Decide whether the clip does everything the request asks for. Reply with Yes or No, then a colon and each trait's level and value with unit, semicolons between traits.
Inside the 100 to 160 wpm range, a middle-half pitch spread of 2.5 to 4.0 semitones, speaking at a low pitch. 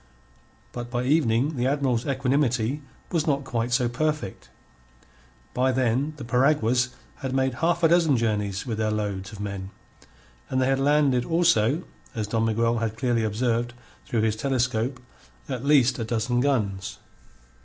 Yes: average, 155 wpm; average, 3.5 semitones; low, 125 Hz